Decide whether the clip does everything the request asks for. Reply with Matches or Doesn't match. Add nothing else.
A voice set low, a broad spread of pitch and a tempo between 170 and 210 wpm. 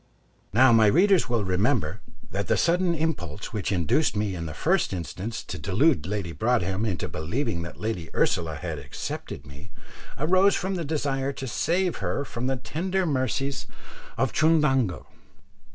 Doesn't match